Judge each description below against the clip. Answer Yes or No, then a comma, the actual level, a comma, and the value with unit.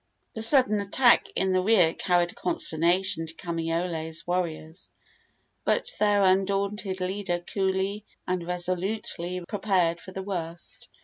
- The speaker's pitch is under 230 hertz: Yes, medium, 185 Hz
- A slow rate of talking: Yes, slow, 120 wpm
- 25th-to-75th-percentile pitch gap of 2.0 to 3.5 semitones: Yes, narrow, 2.5 semitones